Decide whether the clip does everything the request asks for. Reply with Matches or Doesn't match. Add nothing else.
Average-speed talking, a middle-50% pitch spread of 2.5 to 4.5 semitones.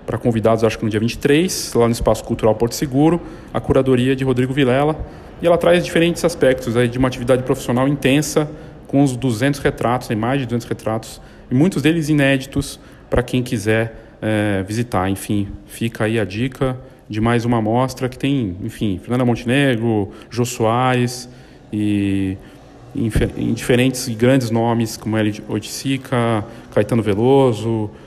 Matches